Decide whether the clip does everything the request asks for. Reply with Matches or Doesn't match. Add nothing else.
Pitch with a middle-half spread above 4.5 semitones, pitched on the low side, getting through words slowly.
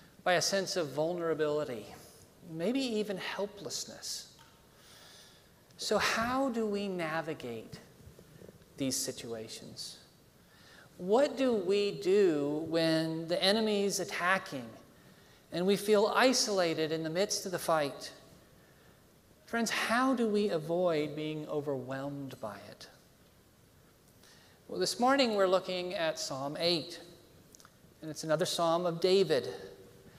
Doesn't match